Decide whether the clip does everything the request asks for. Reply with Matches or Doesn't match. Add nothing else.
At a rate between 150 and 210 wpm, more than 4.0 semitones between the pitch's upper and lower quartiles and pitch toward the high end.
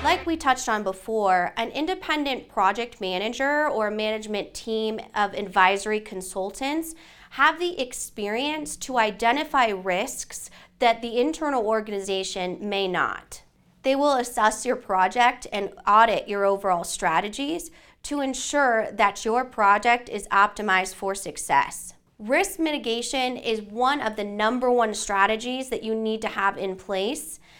Doesn't match